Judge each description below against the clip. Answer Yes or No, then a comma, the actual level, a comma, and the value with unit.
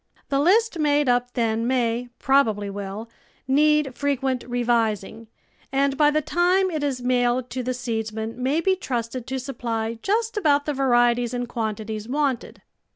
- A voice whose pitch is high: Yes, very high, 250 Hz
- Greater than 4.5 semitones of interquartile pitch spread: No, average, 3.9 semitones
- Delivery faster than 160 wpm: No, average, 155 wpm